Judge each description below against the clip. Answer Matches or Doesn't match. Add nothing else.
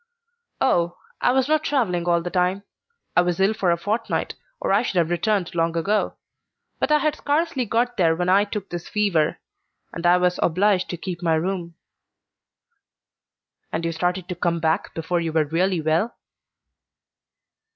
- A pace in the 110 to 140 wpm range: Doesn't match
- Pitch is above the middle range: Doesn't match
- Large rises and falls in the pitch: Doesn't match